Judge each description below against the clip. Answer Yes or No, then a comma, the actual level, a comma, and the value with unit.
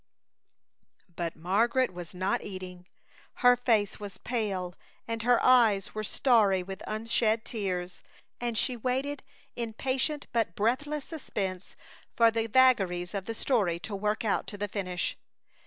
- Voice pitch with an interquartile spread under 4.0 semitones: No, average, 4.3 semitones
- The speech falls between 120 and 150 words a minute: Yes, average, 140 wpm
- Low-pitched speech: No, high, 215 Hz